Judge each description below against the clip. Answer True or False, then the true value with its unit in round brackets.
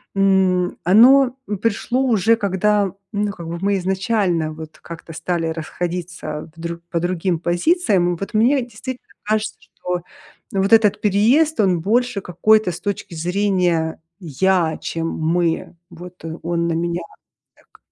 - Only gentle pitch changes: False (3.7 semitones)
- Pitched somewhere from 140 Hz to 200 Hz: True (185 Hz)